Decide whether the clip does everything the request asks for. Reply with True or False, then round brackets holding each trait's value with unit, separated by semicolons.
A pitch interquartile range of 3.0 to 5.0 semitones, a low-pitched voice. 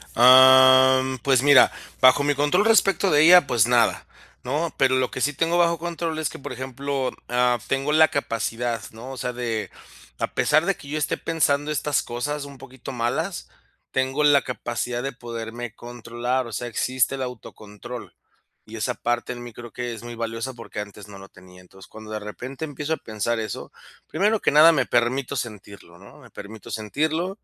True (3.7 semitones; 130 Hz)